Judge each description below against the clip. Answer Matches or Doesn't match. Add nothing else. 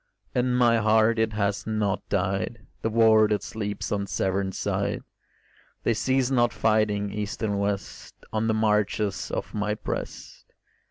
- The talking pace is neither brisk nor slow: Matches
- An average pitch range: Doesn't match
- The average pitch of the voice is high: Doesn't match